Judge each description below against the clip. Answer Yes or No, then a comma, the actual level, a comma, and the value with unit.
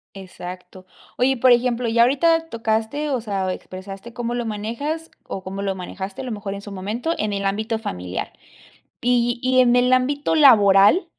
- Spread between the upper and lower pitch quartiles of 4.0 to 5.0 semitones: Yes, average, 4.4 semitones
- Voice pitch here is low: No, high, 225 Hz